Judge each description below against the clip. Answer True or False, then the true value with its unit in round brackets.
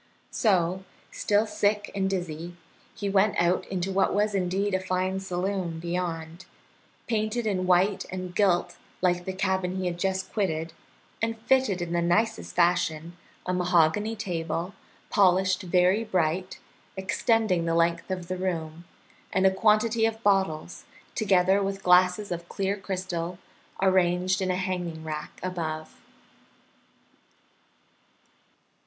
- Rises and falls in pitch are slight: True (2.2 semitones)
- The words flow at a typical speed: False (130 wpm)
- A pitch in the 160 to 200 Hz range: True (185 Hz)